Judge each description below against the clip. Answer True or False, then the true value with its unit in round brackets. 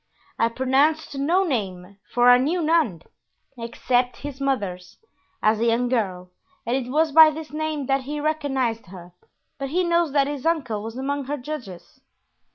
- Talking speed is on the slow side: False (165 wpm)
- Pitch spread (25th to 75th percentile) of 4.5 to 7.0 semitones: True (4.9 semitones)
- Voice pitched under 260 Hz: False (265 Hz)